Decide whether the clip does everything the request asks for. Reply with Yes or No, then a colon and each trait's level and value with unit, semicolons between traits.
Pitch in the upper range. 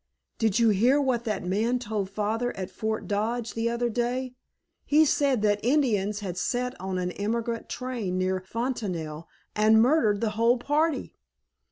Yes: high, 225 Hz